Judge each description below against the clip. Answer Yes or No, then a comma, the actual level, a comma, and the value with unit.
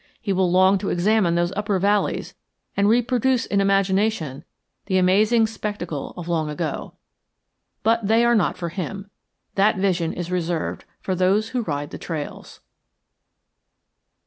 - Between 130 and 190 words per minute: Yes, average, 145 wpm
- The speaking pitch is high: Yes, high, 195 Hz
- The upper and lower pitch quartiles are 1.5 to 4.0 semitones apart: Yes, average, 3.5 semitones